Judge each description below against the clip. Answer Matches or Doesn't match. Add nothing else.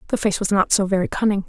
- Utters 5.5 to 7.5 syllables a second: Matches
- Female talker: Matches